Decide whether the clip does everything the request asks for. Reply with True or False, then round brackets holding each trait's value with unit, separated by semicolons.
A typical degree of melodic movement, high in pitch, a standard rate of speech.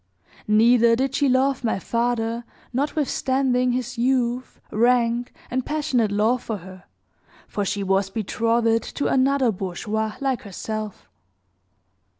False (3.0 semitones; 235 Hz; 120 wpm)